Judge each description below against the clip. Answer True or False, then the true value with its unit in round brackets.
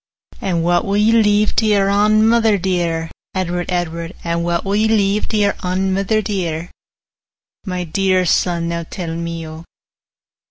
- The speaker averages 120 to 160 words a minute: False (170 wpm)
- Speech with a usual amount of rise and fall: True (3.4 semitones)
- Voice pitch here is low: False (185 Hz)